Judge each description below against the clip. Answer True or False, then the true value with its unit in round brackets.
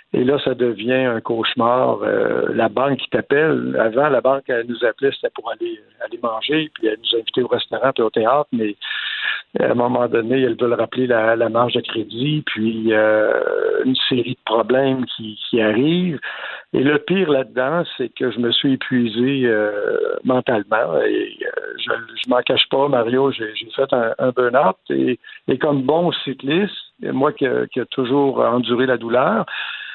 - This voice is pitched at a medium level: False (130 Hz)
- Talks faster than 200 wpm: False (185 wpm)